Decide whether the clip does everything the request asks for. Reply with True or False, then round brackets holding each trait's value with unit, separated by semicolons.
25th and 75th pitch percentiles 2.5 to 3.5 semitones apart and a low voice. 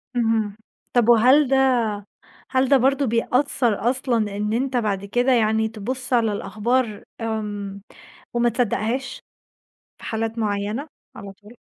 False (3.2 semitones; 230 Hz)